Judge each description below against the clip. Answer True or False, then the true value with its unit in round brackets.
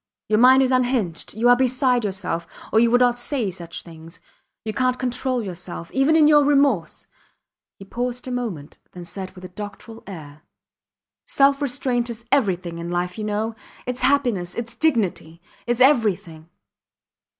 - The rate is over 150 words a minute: True (160 wpm)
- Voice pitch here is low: False (230 Hz)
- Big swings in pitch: True (5.9 semitones)